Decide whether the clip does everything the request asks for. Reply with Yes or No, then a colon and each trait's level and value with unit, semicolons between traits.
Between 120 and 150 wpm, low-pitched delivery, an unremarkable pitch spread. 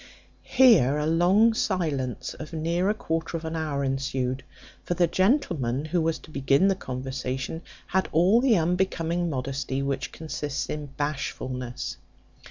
No: average, 145 wpm; medium, 155 Hz; average, 4.6 semitones